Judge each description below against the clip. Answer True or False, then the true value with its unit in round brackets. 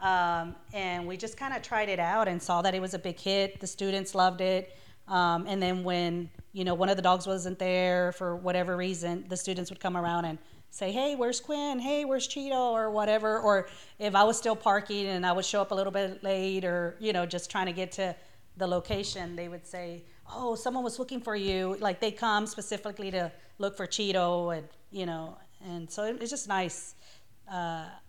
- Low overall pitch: False (190 Hz)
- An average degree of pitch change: True (3.0 semitones)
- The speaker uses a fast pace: True (220 wpm)